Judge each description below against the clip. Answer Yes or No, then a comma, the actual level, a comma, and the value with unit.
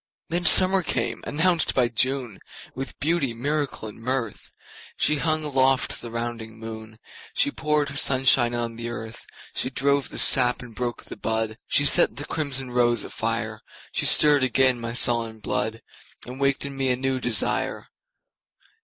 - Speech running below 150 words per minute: Yes, average, 140 wpm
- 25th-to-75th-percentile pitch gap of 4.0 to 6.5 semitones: No, average, 3.3 semitones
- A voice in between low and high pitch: No, low, 130 Hz